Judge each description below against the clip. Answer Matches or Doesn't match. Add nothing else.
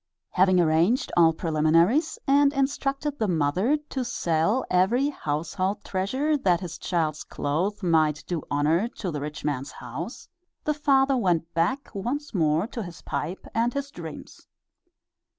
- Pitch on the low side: Doesn't match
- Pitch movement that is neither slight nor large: Doesn't match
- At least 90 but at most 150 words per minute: Matches